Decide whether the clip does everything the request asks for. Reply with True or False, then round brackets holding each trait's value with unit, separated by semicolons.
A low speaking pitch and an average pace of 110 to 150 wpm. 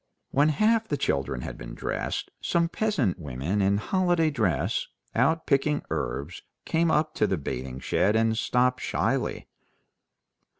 True (115 Hz; 140 wpm)